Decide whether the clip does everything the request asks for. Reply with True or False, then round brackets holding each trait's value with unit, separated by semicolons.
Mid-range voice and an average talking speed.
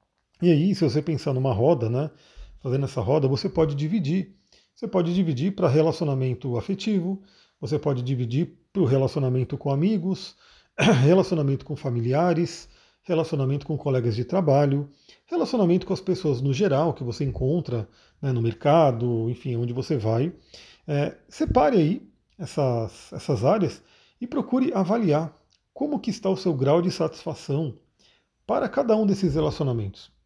True (150 Hz; 145 wpm)